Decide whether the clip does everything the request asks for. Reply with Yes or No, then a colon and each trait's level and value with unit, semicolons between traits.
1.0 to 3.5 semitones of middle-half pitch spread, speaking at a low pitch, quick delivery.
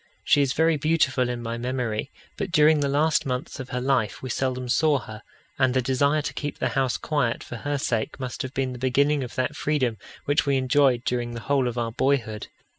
Yes: average, 2.8 semitones; low, 130 Hz; fast, 220 wpm